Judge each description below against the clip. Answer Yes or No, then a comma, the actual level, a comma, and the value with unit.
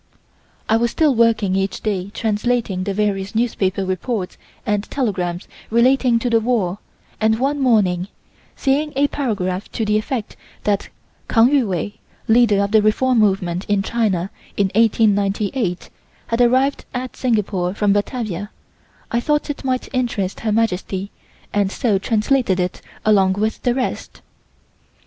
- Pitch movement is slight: No, average, 3.7 semitones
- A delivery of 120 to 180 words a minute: Yes, average, 145 wpm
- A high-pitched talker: Yes, high, 215 Hz